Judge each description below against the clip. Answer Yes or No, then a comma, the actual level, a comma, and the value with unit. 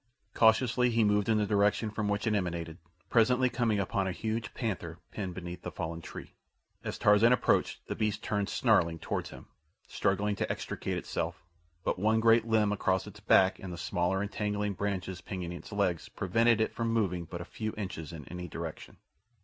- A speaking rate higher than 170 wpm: Yes, average, 185 wpm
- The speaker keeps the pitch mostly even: No, average, 3.8 semitones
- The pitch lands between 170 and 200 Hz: No, low, 100 Hz